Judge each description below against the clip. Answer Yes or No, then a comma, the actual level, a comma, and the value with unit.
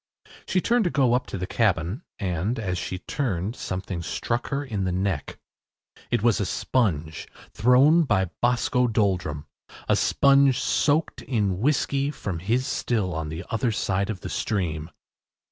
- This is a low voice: Yes, low, 105 Hz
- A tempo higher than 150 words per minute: Yes, average, 160 wpm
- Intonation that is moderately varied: No, wide, 5.7 semitones